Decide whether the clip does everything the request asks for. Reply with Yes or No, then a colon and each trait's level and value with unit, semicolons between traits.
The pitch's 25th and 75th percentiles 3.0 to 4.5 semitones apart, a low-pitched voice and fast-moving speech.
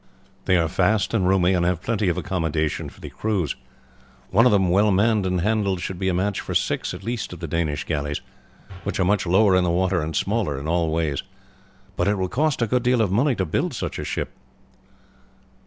Yes: average, 3.5 semitones; very low, 95 Hz; fast, 220 wpm